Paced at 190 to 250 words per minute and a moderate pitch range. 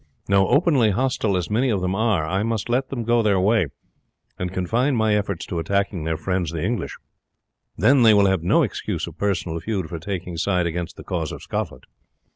Yes: fast, 205 wpm; average, 4.2 semitones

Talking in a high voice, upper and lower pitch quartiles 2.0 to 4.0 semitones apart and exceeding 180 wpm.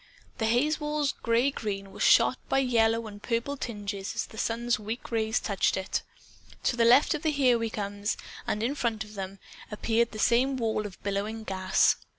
Yes: high, 225 Hz; average, 3.0 semitones; average, 190 wpm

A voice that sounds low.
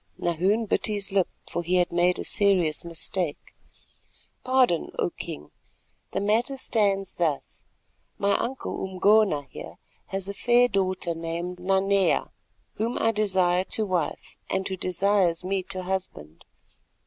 No: high, 190 Hz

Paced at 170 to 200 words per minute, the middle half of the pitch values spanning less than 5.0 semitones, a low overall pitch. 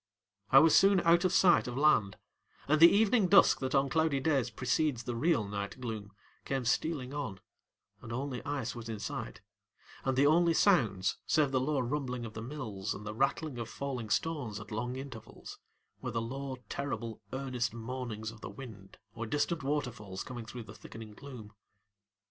Yes: average, 180 wpm; average, 4.5 semitones; low, 130 Hz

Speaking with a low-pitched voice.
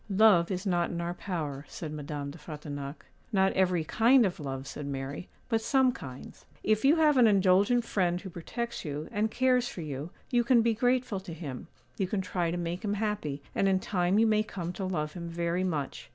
No: medium, 185 Hz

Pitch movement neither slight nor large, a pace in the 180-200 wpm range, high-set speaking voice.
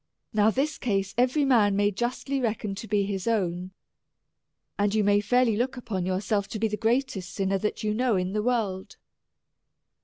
Yes: average, 3.5 semitones; average, 190 wpm; high, 210 Hz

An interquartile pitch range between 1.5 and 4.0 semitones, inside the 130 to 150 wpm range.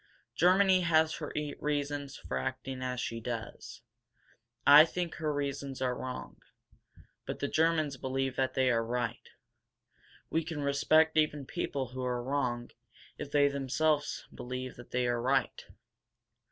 Yes: average, 3.2 semitones; average, 140 wpm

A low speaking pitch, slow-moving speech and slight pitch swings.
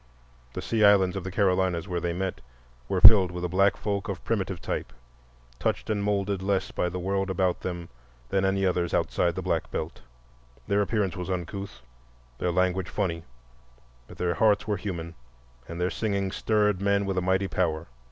No: very low, 95 Hz; average, 180 wpm; narrow, 2.1 semitones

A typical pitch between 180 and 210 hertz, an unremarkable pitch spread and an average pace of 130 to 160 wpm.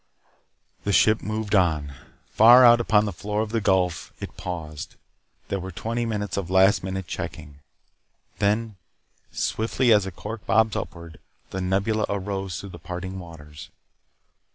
No: low, 100 Hz; average, 3.2 semitones; average, 150 wpm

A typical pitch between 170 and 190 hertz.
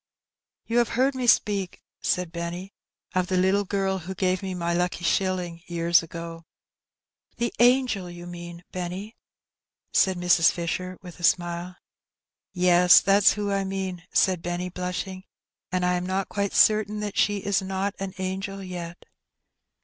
Yes: medium, 185 Hz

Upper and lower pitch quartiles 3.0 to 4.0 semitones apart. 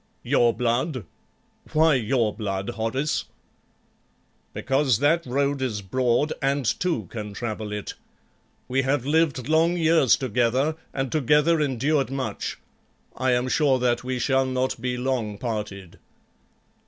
Yes: average, 3.5 semitones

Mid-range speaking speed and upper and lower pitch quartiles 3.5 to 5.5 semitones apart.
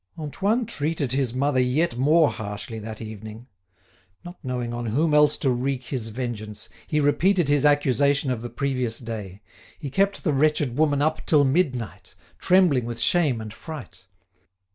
Yes: average, 160 wpm; average, 4.4 semitones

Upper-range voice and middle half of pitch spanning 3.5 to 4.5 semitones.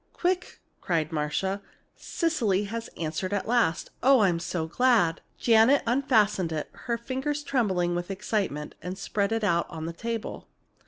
No: high, 200 Hz; wide, 5.5 semitones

